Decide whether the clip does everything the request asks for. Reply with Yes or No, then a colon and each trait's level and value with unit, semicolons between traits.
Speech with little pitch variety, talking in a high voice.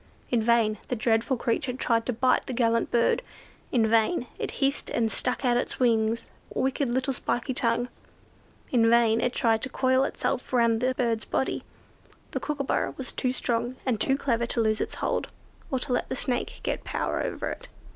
Yes: narrow, 2.1 semitones; high, 240 Hz